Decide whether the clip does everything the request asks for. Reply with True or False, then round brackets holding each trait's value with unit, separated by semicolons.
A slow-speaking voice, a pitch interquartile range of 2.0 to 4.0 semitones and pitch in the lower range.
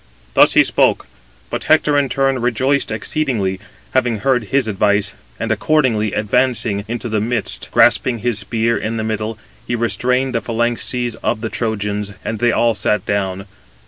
False (160 wpm; 2.8 semitones; 115 Hz)